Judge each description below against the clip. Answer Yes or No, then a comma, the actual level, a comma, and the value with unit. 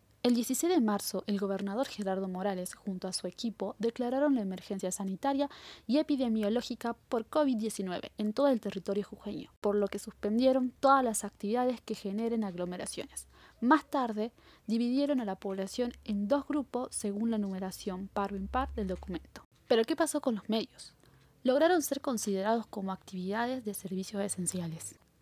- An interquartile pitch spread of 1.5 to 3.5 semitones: No, average, 4.2 semitones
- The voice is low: No, high, 220 Hz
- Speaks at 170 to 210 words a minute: No, average, 160 wpm